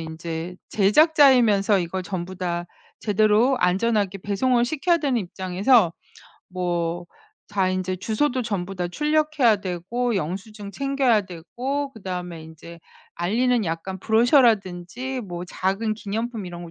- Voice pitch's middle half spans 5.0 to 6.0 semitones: Yes, average, 5.3 semitones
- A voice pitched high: Yes, high, 200 Hz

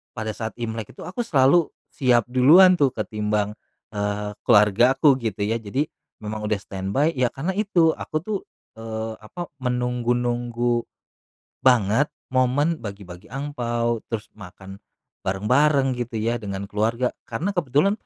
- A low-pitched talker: Yes, low, 120 Hz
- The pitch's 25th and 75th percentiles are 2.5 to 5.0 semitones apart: Yes, average, 4.2 semitones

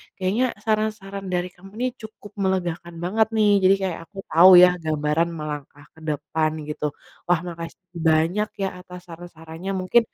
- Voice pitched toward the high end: No, medium, 180 Hz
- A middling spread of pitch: Yes, average, 3.3 semitones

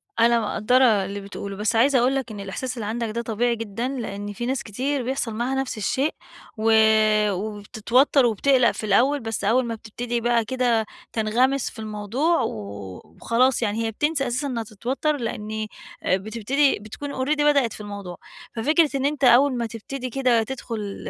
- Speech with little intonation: No, average, 3.5 semitones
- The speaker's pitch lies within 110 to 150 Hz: No, high, 235 Hz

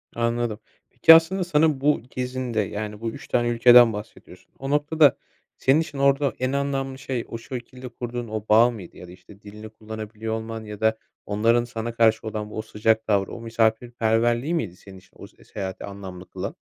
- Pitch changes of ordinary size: Yes, average, 3.1 semitones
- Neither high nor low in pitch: No, low, 115 Hz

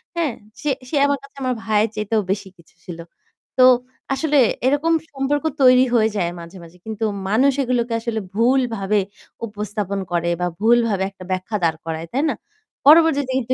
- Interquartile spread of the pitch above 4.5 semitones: Yes, average, 5.2 semitones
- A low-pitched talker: No, high, 225 Hz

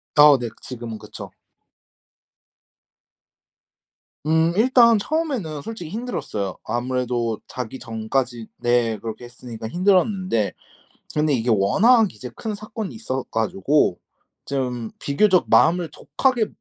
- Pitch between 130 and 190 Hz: Yes, low, 135 Hz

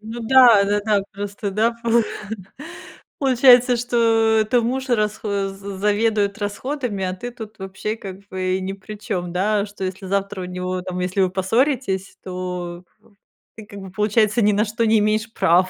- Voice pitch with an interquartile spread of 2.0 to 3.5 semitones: Yes, average, 2.9 semitones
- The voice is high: Yes, high, 205 Hz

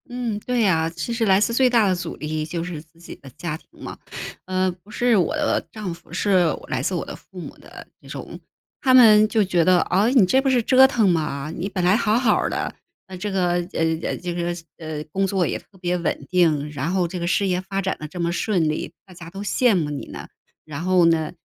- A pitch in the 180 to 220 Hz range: Yes, medium, 185 Hz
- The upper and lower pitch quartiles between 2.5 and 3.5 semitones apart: No, average, 4.0 semitones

